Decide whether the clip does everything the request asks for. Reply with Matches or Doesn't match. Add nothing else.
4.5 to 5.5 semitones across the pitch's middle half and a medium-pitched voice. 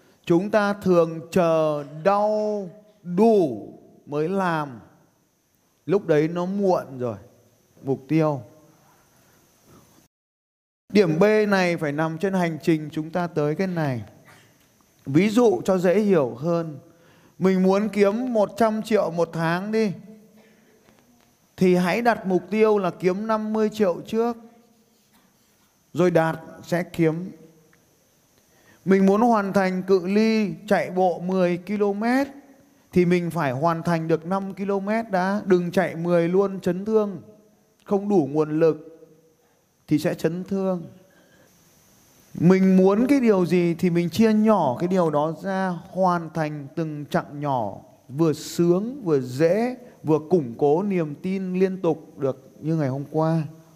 Doesn't match